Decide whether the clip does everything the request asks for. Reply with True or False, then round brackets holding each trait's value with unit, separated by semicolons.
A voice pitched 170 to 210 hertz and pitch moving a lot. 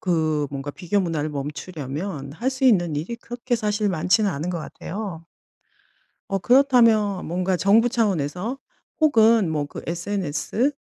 True (185 Hz; 6.1 semitones)